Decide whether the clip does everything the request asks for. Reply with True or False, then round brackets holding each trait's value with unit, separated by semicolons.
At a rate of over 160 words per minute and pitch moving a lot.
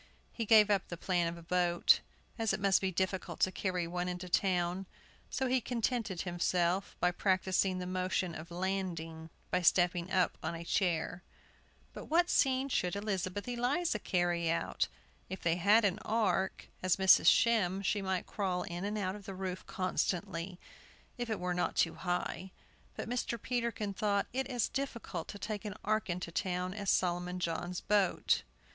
False (175 wpm; 2.9 semitones)